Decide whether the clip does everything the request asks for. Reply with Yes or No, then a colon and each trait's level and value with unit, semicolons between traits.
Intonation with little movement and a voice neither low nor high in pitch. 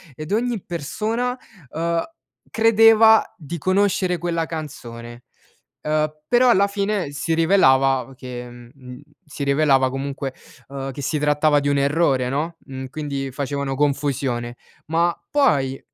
No: average, 4.5 semitones; medium, 150 Hz